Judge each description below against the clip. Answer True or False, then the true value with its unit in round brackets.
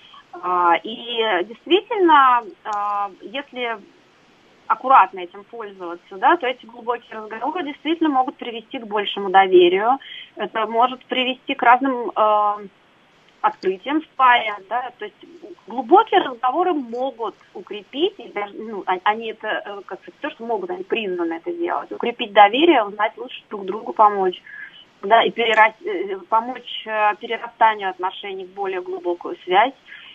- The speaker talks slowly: False (125 wpm)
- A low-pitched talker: False (235 Hz)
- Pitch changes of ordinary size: False (6.8 semitones)